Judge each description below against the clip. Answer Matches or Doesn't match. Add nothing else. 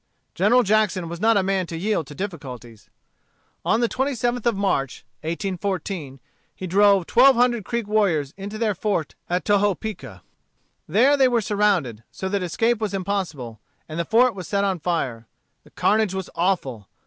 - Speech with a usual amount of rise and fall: Matches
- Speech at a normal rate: Matches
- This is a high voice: Matches